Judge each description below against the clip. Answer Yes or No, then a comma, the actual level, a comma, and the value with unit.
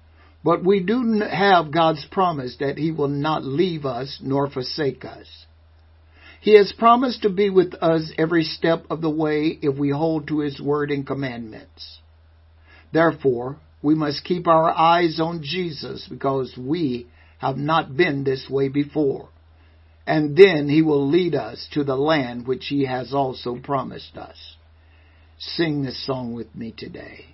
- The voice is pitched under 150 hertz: Yes, medium, 140 Hz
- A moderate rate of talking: Yes, average, 160 wpm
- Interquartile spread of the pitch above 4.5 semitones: Yes, average, 5.1 semitones